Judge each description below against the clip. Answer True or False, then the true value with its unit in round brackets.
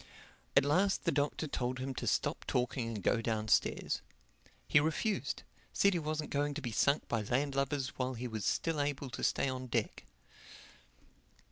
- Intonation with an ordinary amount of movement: True (3.2 semitones)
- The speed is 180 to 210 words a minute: False (160 wpm)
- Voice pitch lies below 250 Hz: True (135 Hz)